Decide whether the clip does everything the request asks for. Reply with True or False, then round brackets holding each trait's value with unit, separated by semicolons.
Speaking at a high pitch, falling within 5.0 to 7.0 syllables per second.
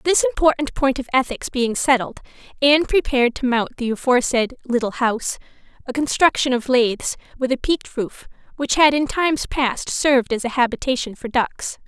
True (260 Hz; 5.5 syllables/s)